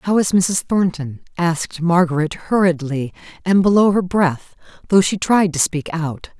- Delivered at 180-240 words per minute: No, average, 160 wpm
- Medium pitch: Yes, medium, 175 Hz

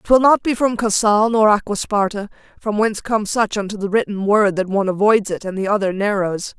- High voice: Yes, high, 205 Hz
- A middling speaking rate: No, fast, 210 wpm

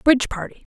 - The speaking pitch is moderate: No, very high, 250 Hz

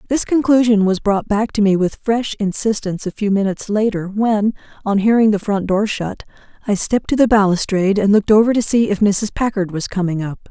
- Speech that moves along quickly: Yes, fast, 210 wpm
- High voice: Yes, high, 210 Hz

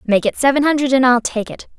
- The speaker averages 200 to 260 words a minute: No, fast, 270 wpm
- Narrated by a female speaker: Yes, female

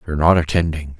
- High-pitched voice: No, very low, 80 Hz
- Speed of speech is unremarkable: Yes, average, 180 wpm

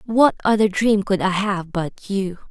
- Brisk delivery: No, average, 190 wpm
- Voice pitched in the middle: No, high, 200 Hz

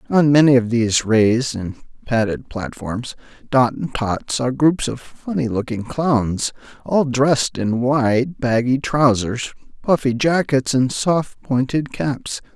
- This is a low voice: Yes, low, 125 Hz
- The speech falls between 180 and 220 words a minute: No, average, 140 wpm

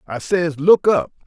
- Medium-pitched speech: Yes, medium, 155 Hz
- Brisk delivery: No, average, 190 wpm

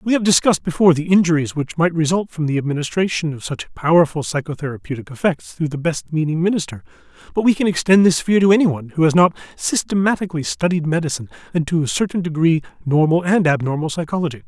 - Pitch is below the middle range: No, medium, 165 Hz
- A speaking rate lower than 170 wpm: No, average, 185 wpm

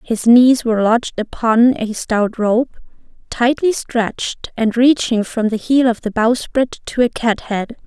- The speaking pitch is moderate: No, high, 235 Hz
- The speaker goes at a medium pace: Yes, average, 160 wpm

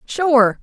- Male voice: No, female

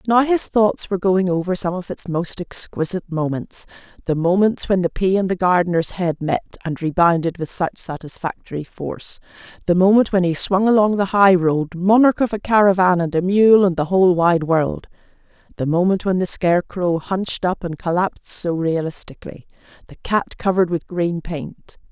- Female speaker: Yes, female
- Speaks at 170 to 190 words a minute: Yes, average, 180 wpm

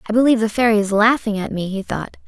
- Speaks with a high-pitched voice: Yes, high, 215 Hz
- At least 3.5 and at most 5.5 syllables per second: No, 7.0 syllables/s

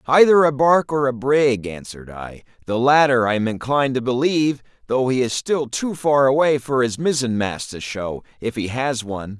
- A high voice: No, low, 130 Hz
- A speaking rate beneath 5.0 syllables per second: No, 5.1 syllables/s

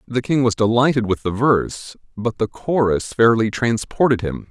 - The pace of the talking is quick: No, average, 175 wpm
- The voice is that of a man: Yes, male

